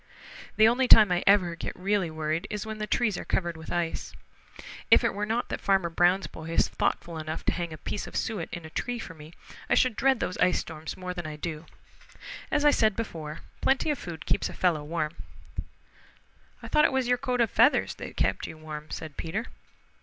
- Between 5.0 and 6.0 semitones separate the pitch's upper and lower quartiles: Yes, wide, 5.4 semitones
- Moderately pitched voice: Yes, medium, 180 Hz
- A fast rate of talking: Yes, fast, 220 wpm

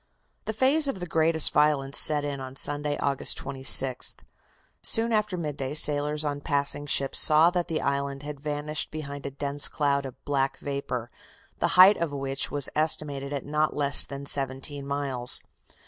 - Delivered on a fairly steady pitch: Yes, narrow, 1.7 semitones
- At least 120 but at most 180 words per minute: Yes, average, 160 wpm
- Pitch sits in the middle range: Yes, medium, 145 Hz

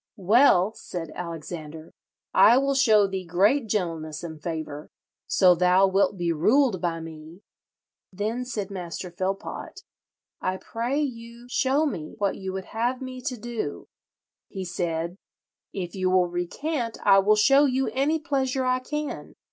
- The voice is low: No, high, 195 Hz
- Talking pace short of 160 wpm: Yes, average, 150 wpm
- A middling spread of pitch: No, wide, 6.4 semitones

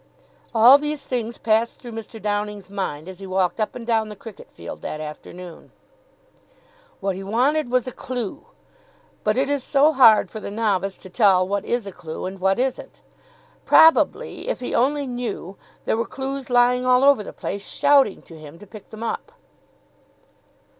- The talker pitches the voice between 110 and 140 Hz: No, high, 225 Hz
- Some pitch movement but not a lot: Yes, average, 4.5 semitones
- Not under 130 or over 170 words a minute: No, average, 180 wpm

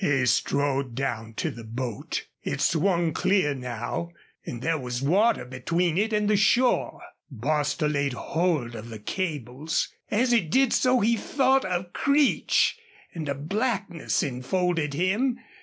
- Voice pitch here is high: No, medium, 160 Hz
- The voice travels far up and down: Yes, wide, 7.5 semitones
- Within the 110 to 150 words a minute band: Yes, average, 145 wpm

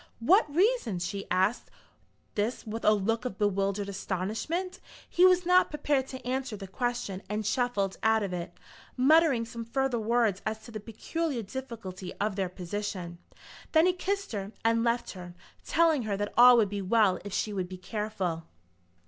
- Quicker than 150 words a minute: Yes, average, 175 wpm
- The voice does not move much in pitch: No, average, 4.8 semitones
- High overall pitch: Yes, high, 220 Hz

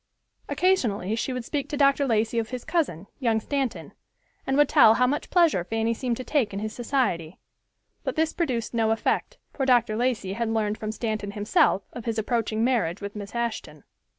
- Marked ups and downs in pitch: No, average, 3.5 semitones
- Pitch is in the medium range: No, high, 230 Hz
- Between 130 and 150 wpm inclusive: No, average, 190 wpm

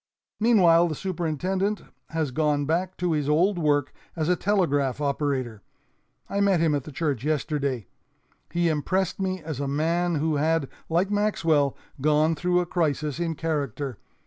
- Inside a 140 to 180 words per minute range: Yes, average, 155 wpm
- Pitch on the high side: No, medium, 160 Hz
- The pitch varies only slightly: No, average, 3.5 semitones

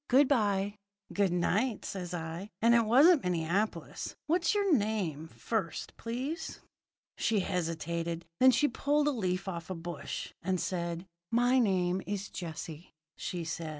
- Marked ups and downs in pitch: Yes, wide, 5.7 semitones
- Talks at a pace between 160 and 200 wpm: No, average, 145 wpm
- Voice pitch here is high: Yes, high, 195 Hz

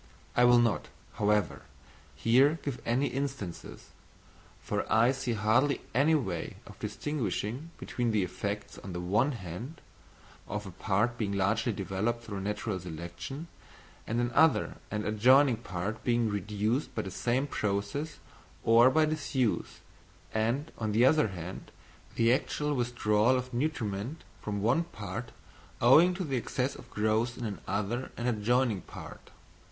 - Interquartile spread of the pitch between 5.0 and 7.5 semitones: No, average, 4.2 semitones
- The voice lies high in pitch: No, low, 115 Hz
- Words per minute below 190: Yes, average, 140 wpm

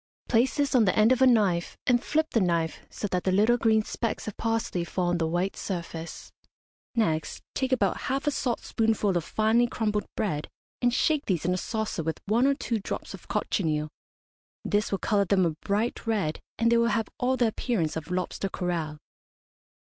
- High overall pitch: Yes, high, 210 Hz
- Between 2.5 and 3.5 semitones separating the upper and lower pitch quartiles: No, average, 4.9 semitones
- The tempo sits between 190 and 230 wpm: Yes, average, 195 wpm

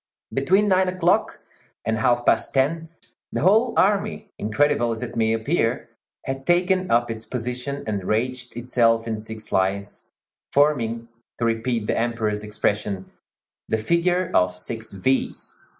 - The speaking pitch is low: Yes, low, 120 Hz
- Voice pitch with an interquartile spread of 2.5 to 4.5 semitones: No, average, 5.0 semitones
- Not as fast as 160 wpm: Yes, average, 140 wpm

